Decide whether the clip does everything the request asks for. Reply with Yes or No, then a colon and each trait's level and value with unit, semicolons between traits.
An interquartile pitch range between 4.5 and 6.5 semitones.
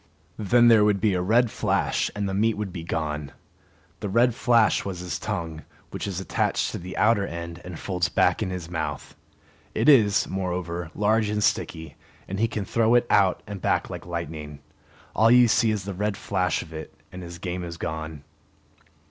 No: average, 3.9 semitones